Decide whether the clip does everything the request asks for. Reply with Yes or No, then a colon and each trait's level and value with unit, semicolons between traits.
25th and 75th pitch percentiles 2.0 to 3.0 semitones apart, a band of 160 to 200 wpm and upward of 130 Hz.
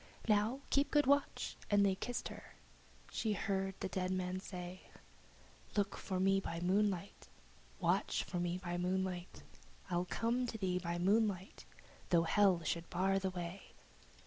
No: narrow, 2.4 semitones; average, 150 wpm; high, 190 Hz